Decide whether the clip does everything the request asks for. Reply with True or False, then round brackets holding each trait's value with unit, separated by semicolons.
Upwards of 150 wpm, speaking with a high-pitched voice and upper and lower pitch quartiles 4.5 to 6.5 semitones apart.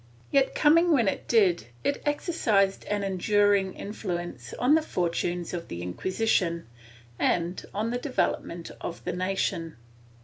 False (135 wpm; 195 Hz; 4.9 semitones)